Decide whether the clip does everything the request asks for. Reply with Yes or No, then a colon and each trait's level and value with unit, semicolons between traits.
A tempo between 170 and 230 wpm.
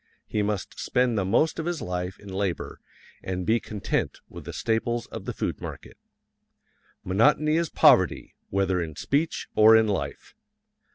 No: average, 160 wpm